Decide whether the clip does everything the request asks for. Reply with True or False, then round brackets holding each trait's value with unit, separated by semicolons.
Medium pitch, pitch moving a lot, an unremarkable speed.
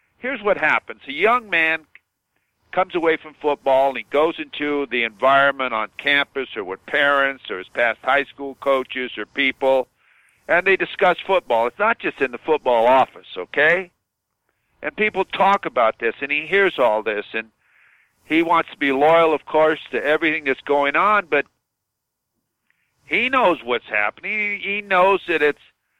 False (150 Hz; 4.7 semitones; 170 wpm)